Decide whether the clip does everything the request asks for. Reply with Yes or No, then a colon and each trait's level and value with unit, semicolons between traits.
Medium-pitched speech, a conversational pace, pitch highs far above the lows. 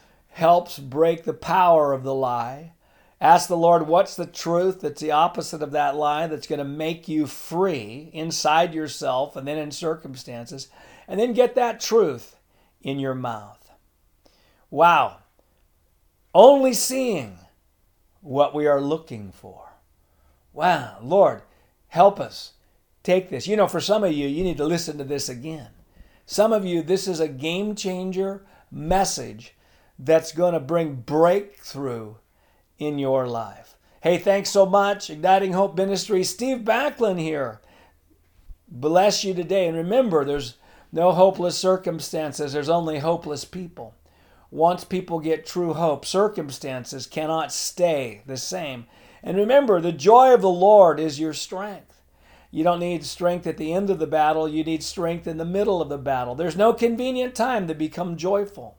Yes: medium, 160 Hz; average, 155 wpm; wide, 5.7 semitones